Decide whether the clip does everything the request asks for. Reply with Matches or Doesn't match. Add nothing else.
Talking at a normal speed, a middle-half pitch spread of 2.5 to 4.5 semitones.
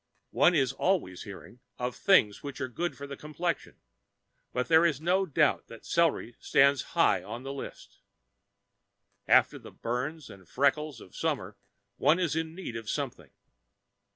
Doesn't match